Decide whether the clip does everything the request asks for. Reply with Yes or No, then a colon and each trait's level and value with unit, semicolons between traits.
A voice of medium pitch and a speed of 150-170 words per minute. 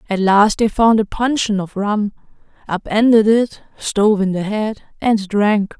No: high, 210 Hz; average, 165 wpm